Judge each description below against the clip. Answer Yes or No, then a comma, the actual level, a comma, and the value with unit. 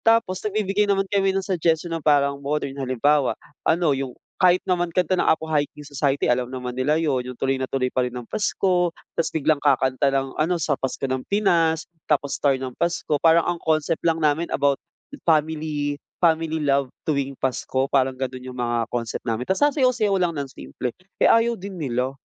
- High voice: No, medium, 150 Hz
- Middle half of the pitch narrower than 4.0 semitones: No, average, 4.4 semitones